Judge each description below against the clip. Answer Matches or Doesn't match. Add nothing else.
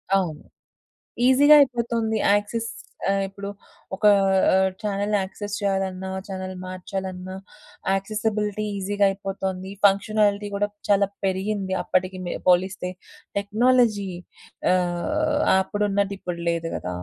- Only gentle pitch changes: Matches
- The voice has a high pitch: Matches